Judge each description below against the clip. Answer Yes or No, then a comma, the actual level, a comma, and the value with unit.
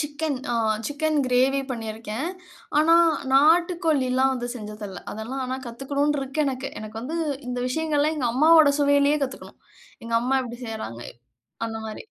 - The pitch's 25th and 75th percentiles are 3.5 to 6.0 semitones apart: Yes, average, 4.0 semitones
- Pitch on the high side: Yes, very high, 270 Hz